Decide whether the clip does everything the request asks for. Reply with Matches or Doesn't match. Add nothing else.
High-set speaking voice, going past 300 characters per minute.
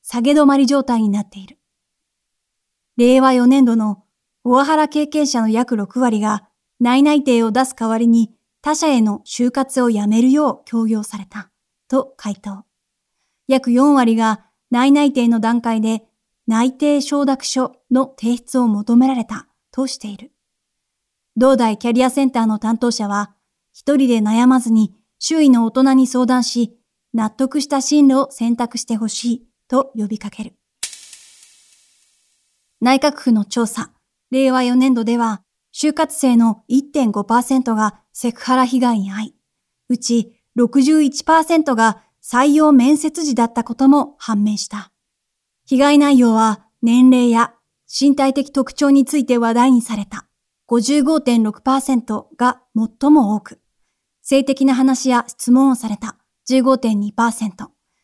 Doesn't match